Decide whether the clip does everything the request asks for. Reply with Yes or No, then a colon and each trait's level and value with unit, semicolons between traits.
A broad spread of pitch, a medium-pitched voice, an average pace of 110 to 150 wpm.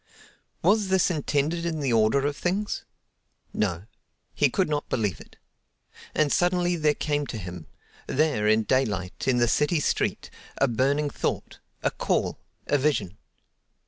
Yes: wide, 6.4 semitones; medium, 145 Hz; average, 140 wpm